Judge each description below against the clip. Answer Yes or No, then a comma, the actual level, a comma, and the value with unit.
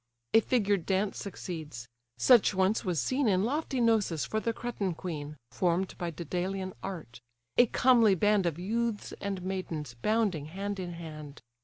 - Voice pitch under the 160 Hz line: No, high, 190 Hz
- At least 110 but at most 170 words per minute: Yes, average, 155 wpm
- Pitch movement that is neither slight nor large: Yes, average, 4.3 semitones